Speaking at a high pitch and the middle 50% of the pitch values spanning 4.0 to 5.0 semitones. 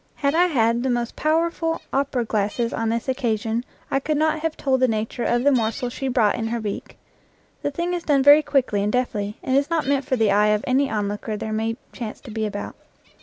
Yes: high, 245 Hz; average, 4.3 semitones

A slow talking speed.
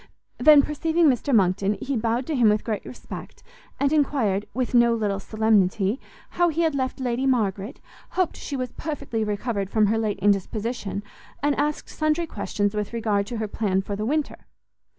No: average, 175 wpm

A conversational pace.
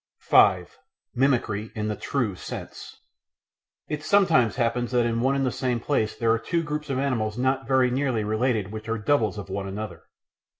Yes: average, 185 wpm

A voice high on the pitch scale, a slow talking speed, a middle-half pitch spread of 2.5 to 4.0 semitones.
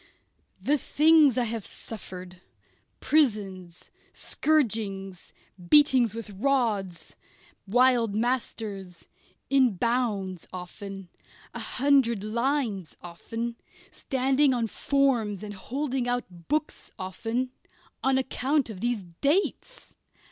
No: high, 230 Hz; slow, 95 wpm; wide, 5.5 semitones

